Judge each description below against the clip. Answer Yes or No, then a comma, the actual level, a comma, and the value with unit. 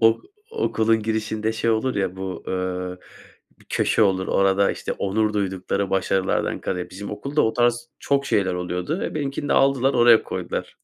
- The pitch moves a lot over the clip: No, average, 4.0 semitones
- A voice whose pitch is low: Yes, low, 105 Hz